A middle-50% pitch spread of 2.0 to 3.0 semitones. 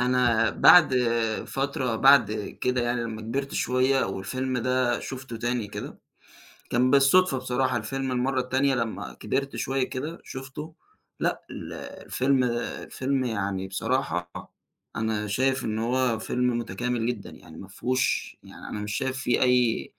Yes: average, 2.7 semitones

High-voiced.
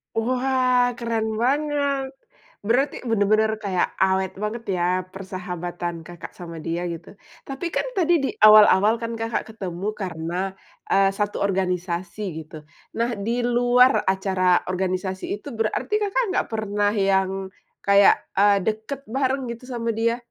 Yes: high, 210 Hz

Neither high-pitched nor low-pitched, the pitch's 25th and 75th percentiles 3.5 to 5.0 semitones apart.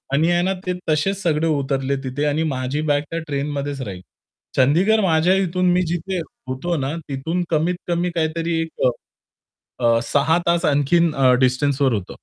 Yes: medium, 155 Hz; average, 3.8 semitones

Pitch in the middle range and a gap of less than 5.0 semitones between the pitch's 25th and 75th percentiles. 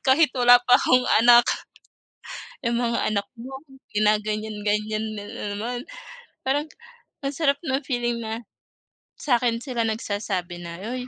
No: high, 235 Hz; average, 3.0 semitones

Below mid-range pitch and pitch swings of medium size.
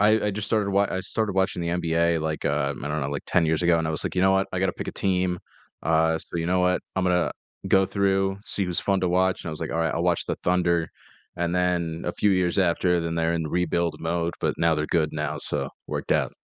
No: very low, 85 Hz; narrow, 2.3 semitones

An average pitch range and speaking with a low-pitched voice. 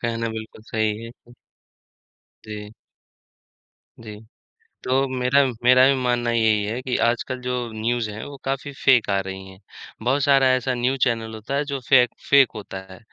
Yes: average, 3.1 semitones; low, 120 Hz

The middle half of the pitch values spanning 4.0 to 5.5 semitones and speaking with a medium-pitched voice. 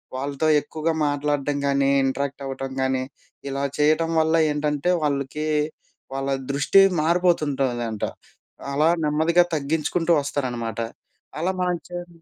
No: average, 2.7 semitones; medium, 145 Hz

